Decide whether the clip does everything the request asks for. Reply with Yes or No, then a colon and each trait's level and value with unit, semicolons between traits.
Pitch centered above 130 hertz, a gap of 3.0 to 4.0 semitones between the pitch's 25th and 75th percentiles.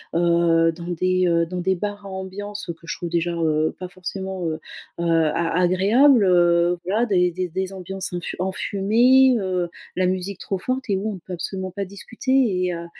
No: medium, 185 Hz; narrow, 2.4 semitones